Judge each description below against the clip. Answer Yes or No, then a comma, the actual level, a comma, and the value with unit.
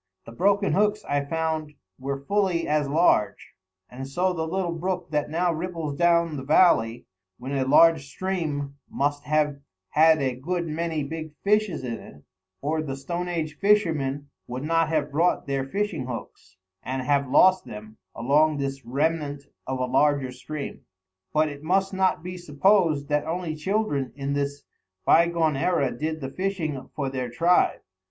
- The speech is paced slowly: No, average, 165 wpm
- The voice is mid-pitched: Yes, medium, 155 Hz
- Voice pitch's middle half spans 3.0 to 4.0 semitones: Yes, average, 3.7 semitones